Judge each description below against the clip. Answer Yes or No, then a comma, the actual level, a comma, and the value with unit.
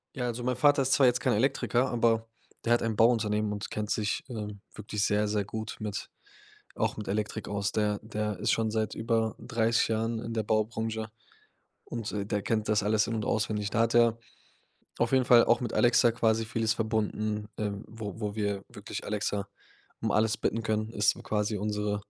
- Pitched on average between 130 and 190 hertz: No, low, 110 Hz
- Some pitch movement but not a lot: No, narrow, 1.6 semitones